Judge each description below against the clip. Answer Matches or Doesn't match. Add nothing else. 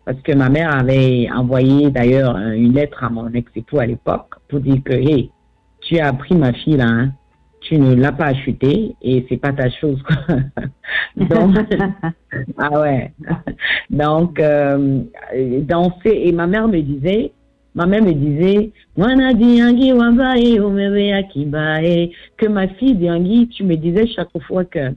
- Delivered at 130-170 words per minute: Matches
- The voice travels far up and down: Matches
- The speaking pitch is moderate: Matches